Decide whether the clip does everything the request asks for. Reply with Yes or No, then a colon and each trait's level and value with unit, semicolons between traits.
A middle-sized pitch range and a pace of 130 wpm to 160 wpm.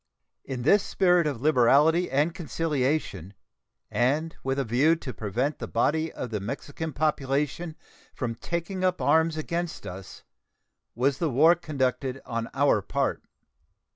Yes: average, 4.2 semitones; average, 140 wpm